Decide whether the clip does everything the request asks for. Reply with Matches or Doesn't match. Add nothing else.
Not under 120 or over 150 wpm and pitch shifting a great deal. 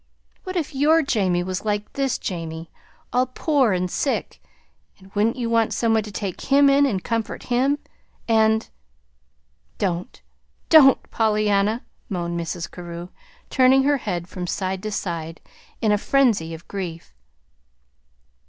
Matches